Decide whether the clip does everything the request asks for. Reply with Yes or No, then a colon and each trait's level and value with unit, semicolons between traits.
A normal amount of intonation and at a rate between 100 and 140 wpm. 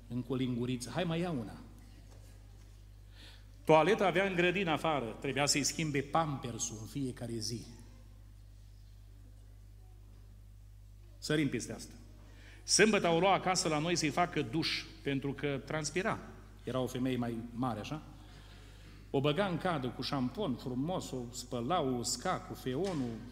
No: wide, 6.5 semitones; average, 135 wpm